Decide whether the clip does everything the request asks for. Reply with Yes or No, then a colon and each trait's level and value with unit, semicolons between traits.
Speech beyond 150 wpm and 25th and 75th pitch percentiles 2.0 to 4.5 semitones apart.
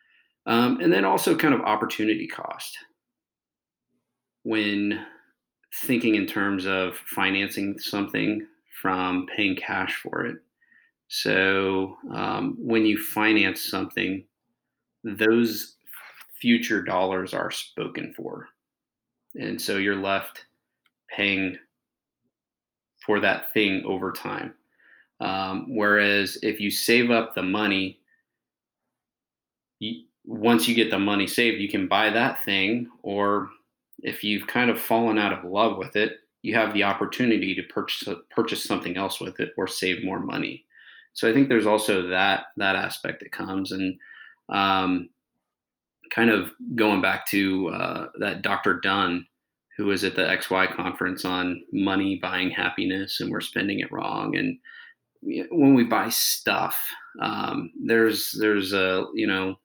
No: slow, 135 wpm; average, 2.9 semitones